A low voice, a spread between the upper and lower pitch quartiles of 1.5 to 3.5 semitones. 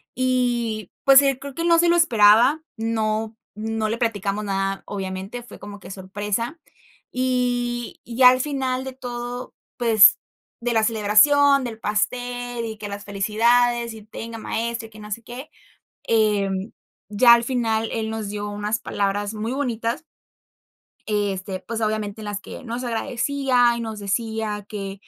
No: high, 225 Hz; average, 2.8 semitones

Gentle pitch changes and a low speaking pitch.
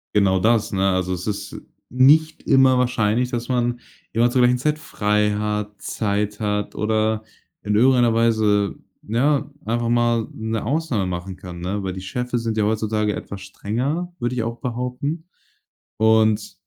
No: average, 3.1 semitones; low, 110 Hz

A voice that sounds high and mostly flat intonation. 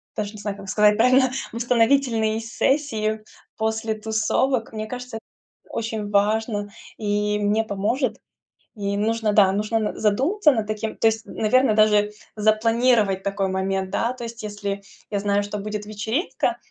Yes: high, 215 Hz; narrow, 1.7 semitones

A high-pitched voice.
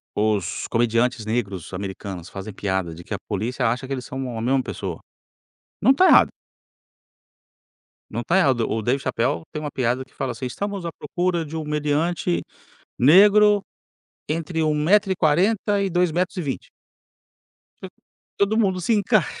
No: medium, 140 Hz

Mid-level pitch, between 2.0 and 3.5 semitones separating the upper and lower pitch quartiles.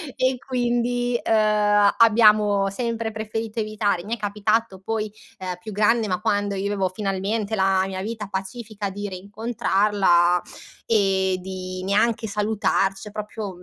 No: high, 210 Hz; narrow, 2.5 semitones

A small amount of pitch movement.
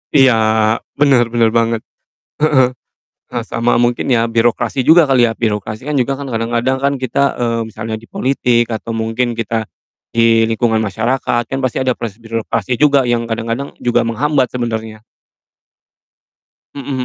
Yes: narrow, 2.3 semitones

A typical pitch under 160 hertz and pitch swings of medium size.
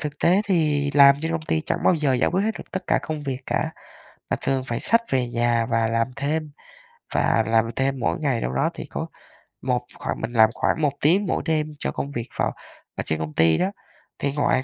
Yes: medium, 140 Hz; average, 4.9 semitones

